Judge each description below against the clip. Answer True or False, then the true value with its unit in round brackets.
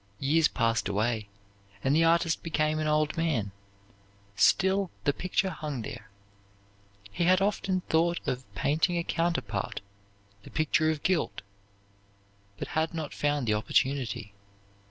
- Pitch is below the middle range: False (155 Hz)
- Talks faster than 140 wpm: False (135 wpm)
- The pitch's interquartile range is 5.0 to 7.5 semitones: True (5.3 semitones)